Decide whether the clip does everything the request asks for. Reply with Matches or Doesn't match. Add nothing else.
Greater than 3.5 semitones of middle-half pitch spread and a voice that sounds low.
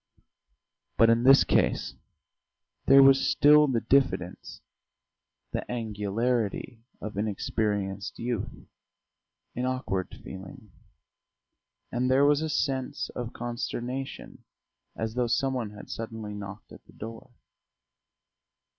Matches